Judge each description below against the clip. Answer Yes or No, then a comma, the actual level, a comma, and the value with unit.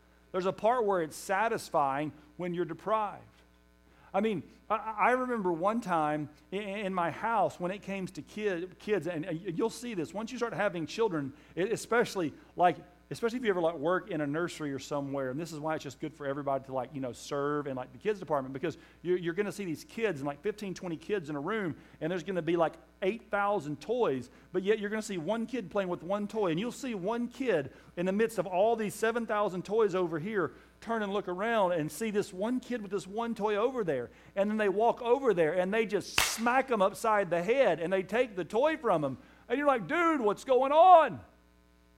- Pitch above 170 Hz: Yes, medium, 185 Hz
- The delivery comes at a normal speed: No, fast, 225 wpm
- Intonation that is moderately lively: No, wide, 5.7 semitones